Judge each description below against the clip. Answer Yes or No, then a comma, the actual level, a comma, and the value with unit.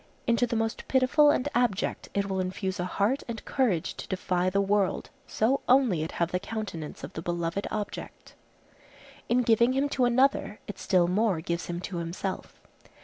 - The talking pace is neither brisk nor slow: Yes, average, 180 wpm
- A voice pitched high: Yes, high, 200 Hz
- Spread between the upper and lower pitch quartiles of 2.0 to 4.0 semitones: No, average, 5.0 semitones